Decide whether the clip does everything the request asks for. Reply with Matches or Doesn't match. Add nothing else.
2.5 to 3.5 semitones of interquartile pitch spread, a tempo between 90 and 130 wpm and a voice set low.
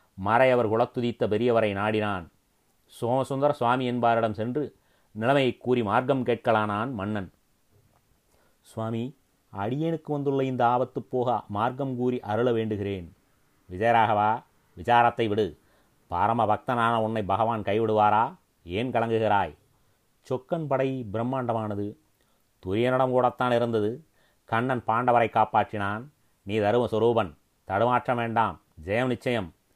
Matches